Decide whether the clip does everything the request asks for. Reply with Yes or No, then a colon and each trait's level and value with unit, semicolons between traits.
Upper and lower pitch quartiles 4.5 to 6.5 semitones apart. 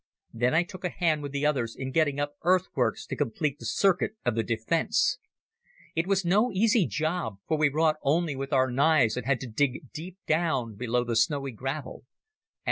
Yes: average, 4.8 semitones